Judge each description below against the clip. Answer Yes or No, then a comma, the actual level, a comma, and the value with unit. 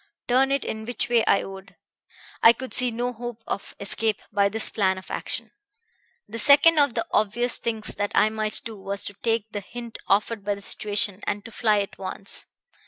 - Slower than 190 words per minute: No, average, 195 wpm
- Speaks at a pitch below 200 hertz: No, high, 220 Hz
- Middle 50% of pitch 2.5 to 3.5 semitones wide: Yes, average, 2.9 semitones